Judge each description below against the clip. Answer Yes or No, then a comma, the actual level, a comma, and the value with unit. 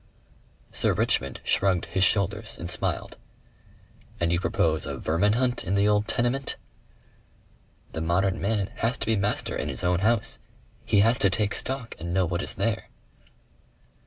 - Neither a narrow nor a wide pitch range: Yes, average, 4.5 semitones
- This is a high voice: No, low, 100 Hz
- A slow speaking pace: No, average, 160 wpm